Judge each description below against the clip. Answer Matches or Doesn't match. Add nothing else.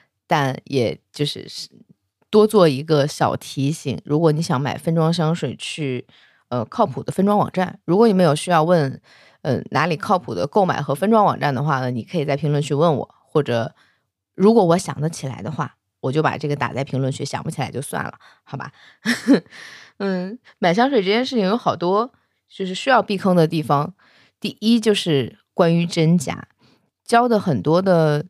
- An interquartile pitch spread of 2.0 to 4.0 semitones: Doesn't match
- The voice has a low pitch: Doesn't match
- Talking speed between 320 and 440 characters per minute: Doesn't match